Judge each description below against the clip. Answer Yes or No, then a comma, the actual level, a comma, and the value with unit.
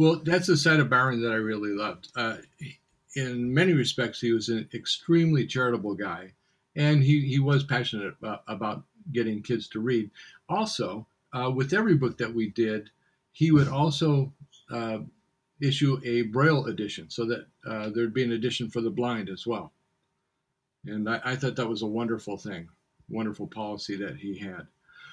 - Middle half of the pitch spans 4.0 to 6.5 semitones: Yes, average, 4.3 semitones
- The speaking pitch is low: Yes, low, 120 Hz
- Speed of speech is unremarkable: Yes, average, 175 wpm